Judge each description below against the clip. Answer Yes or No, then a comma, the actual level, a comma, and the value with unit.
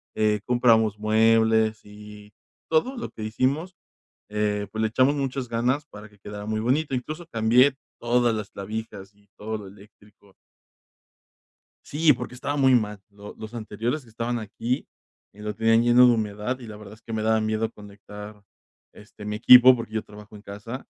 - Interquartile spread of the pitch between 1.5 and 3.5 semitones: Yes, average, 2.8 semitones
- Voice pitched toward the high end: No, low, 110 Hz